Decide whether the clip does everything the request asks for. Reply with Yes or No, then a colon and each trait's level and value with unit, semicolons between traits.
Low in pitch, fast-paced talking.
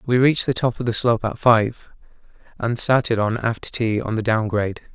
Yes: low, 115 Hz; fast, 220 wpm